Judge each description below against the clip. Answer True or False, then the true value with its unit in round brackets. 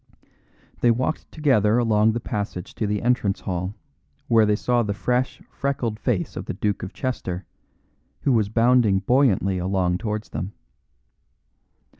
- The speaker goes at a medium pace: True (145 wpm)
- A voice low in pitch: True (110 Hz)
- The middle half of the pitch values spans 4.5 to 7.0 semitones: False (3.8 semitones)